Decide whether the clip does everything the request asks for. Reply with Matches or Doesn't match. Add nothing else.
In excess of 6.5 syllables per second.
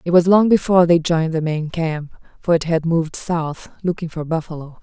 Doesn't match